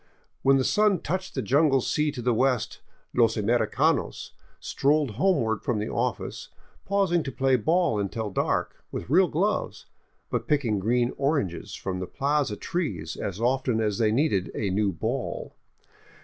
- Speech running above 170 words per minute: No, average, 165 wpm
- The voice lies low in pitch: Yes, low, 125 Hz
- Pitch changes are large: Yes, wide, 5.9 semitones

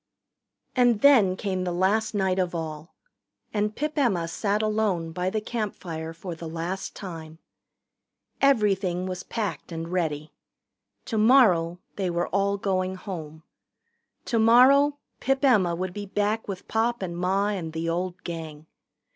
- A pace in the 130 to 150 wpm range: Yes, average, 140 wpm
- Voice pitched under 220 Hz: Yes, high, 190 Hz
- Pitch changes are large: No, average, 4.0 semitones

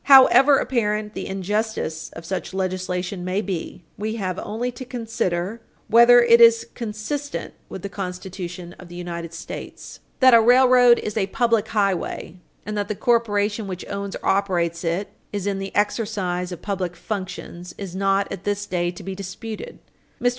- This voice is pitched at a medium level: No, high, 200 Hz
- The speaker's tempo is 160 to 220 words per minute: Yes, average, 170 wpm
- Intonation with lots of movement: No, average, 3.8 semitones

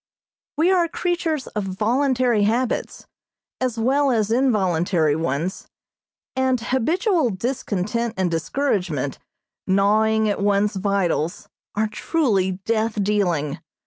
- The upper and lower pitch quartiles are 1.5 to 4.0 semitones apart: No, average, 5.3 semitones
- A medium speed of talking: No, slow, 105 wpm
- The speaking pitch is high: Yes, high, 215 Hz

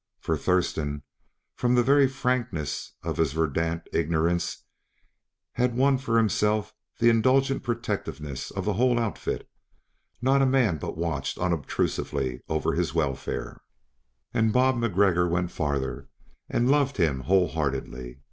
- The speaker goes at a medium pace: No, slow, 130 wpm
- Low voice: Yes, very low, 90 Hz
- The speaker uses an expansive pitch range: Yes, wide, 7.6 semitones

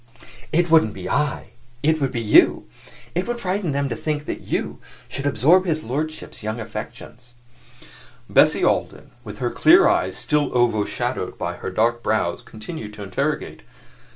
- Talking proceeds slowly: No, average, 155 wpm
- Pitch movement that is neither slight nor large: No, wide, 6.2 semitones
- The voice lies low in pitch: Yes, low, 130 Hz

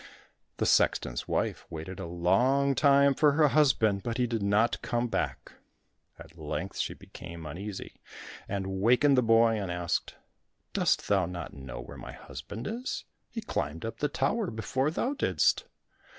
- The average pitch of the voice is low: Yes, low, 115 Hz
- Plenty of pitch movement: Yes, wide, 7.7 semitones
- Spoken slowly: No, average, 160 wpm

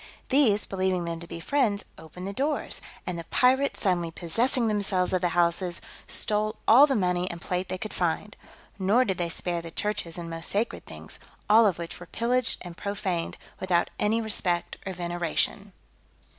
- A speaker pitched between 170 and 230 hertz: Yes, medium, 185 Hz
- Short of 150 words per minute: No, average, 180 wpm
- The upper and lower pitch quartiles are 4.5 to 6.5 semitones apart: No, average, 3.7 semitones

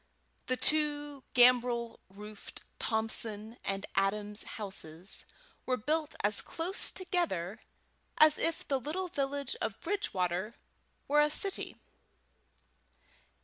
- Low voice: No, high, 245 Hz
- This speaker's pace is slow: Yes, slow, 105 wpm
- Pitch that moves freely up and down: Yes, wide, 6.3 semitones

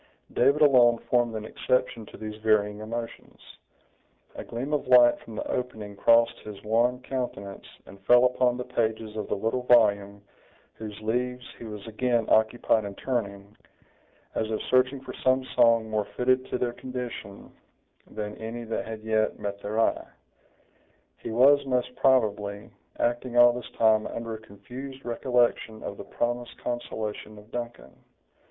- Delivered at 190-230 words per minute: No, average, 155 wpm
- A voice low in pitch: Yes, low, 115 Hz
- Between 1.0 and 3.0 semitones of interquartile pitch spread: Yes, narrow, 2.5 semitones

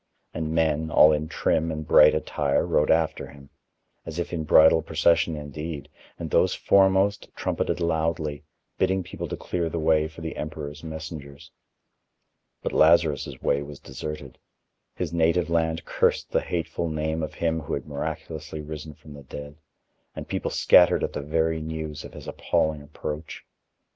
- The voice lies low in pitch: Yes, very low, 80 Hz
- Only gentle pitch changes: Yes, narrow, 1.5 semitones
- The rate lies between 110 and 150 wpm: No, average, 160 wpm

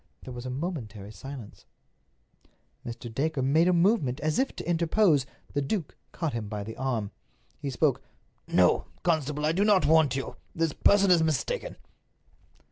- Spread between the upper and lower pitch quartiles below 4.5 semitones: No, average, 5.0 semitones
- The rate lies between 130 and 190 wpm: Yes, average, 160 wpm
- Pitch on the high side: No, medium, 150 Hz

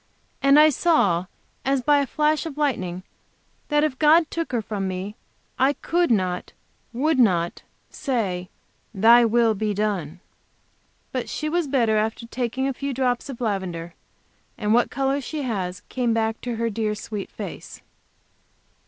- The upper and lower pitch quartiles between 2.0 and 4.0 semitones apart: No, average, 5.2 semitones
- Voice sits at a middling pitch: No, high, 235 Hz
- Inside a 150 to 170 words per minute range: Yes, average, 155 wpm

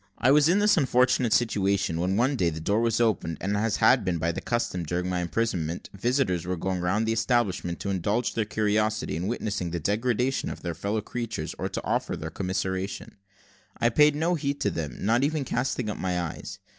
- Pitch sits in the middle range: No, low, 105 Hz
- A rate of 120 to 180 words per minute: No, fast, 205 wpm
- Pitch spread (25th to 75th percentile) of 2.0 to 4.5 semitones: No, average, 5.1 semitones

